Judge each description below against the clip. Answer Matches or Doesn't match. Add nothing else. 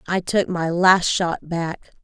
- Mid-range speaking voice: Matches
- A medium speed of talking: Matches